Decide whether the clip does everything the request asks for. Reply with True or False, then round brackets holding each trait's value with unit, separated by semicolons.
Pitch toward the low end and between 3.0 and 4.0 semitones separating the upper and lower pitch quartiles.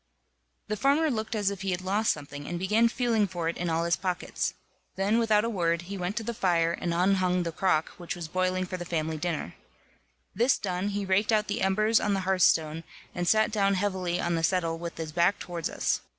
False (185 Hz; 3.4 semitones)